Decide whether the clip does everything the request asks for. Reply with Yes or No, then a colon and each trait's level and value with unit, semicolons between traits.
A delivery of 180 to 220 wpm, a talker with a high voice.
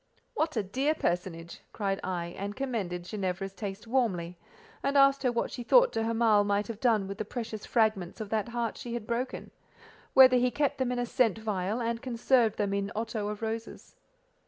Yes: average, 190 wpm; high, 225 Hz